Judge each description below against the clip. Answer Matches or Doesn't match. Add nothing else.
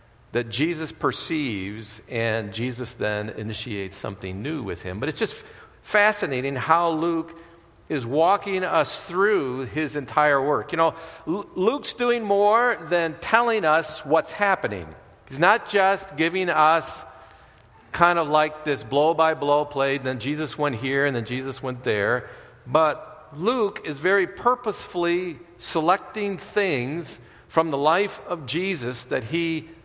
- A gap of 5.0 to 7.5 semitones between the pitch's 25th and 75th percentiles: Matches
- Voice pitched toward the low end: Doesn't match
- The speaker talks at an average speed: Matches